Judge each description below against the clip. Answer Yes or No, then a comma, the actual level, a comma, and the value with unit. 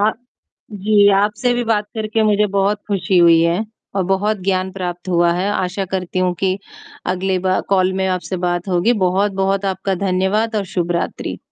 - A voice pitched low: No, high, 190 Hz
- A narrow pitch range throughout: Yes, narrow, 2.0 semitones